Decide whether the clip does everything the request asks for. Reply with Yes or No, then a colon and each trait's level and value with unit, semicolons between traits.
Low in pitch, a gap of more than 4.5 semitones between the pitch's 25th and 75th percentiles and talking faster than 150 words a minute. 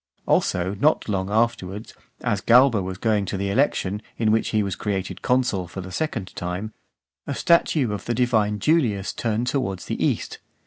No: low, 105 Hz; average, 3.8 semitones; average, 175 wpm